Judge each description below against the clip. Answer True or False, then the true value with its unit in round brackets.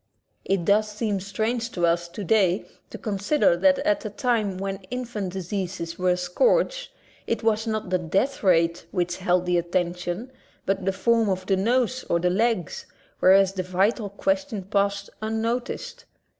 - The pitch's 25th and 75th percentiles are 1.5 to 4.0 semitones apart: True (3.6 semitones)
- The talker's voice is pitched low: False (195 Hz)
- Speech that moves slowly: False (165 wpm)